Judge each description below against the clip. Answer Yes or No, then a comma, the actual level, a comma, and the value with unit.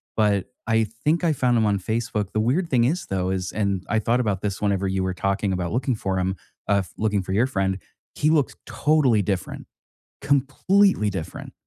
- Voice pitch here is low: Yes, low, 105 Hz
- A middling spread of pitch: Yes, average, 4.8 semitones